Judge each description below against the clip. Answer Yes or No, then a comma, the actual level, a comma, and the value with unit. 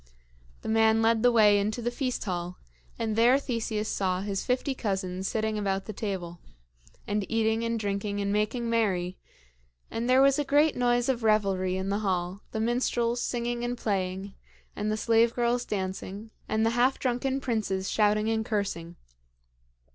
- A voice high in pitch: Yes, high, 220 Hz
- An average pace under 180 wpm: Yes, average, 170 wpm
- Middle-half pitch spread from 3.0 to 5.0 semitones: Yes, average, 3.3 semitones